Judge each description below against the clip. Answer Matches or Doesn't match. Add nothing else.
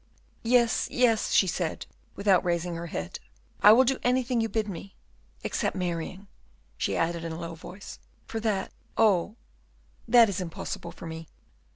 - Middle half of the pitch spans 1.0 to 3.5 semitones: Doesn't match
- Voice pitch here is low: Doesn't match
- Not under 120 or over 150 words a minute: Doesn't match